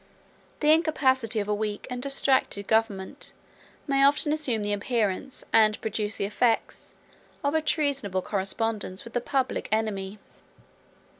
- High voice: Yes, high, 225 Hz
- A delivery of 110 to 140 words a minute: Yes, slow, 135 wpm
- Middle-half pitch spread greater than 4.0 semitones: Yes, average, 4.8 semitones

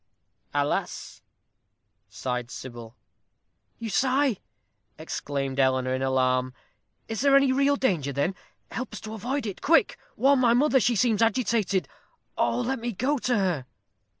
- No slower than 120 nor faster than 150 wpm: Yes, average, 140 wpm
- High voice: Yes, high, 220 Hz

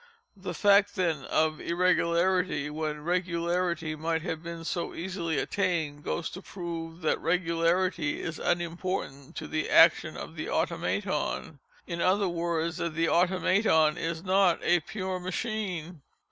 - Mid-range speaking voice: Yes, medium, 170 Hz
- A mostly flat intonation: Yes, narrow, 2.2 semitones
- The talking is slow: Yes, slow, 130 wpm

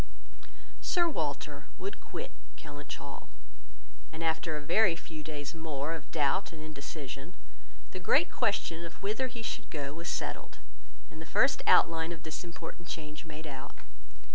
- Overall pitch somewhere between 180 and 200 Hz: No, medium, 160 Hz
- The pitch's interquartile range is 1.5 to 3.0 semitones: Yes, narrow, 2.4 semitones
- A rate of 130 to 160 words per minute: Yes, average, 155 wpm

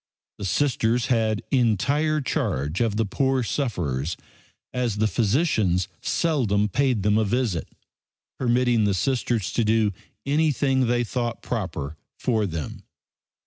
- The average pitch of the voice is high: No, low, 115 Hz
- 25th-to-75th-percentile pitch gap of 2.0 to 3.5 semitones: No, average, 4.2 semitones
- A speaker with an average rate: No, slow, 125 wpm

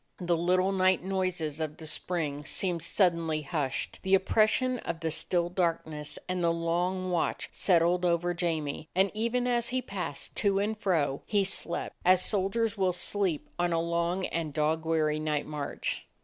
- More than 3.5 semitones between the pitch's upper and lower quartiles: No, average, 2.9 semitones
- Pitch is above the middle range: No, medium, 175 Hz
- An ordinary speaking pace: Yes, average, 170 wpm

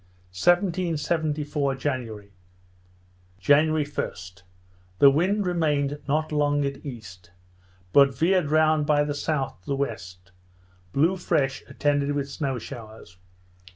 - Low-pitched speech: No, medium, 145 Hz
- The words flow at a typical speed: No, slow, 115 wpm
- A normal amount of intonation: Yes, average, 3.0 semitones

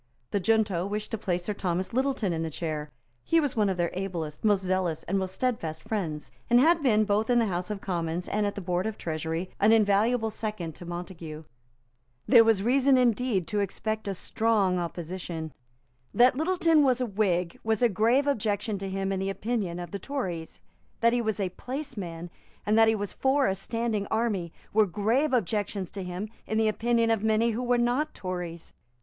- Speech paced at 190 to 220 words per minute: Yes, average, 200 wpm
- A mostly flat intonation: No, average, 4.4 semitones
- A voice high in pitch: Yes, high, 205 Hz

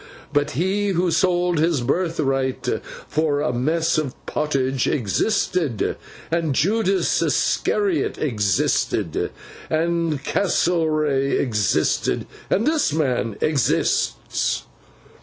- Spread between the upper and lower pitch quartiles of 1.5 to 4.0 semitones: No, average, 4.6 semitones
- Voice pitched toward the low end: No, medium, 155 Hz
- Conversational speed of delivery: No, slow, 90 wpm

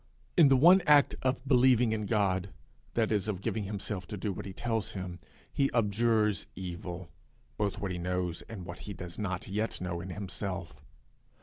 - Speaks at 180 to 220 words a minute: Yes, average, 185 wpm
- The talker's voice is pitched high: No, low, 100 Hz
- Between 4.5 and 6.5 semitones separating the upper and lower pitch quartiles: No, average, 3.7 semitones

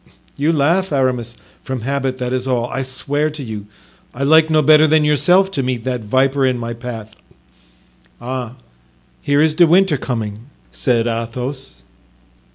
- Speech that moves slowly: No, average, 160 wpm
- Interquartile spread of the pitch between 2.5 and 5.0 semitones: Yes, average, 4.0 semitones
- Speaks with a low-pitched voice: Yes, low, 130 Hz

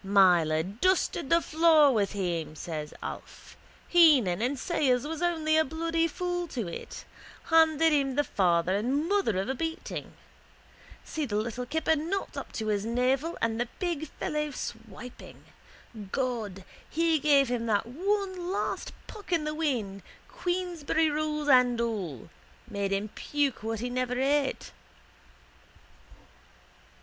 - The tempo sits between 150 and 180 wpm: No, average, 140 wpm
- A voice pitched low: No, very high, 270 Hz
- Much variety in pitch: Yes, wide, 6.7 semitones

